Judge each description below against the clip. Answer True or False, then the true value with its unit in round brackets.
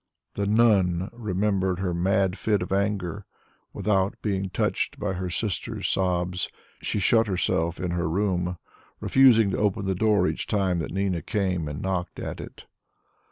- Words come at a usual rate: True (160 wpm)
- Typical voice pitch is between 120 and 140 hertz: False (95 Hz)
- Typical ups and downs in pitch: False (2.3 semitones)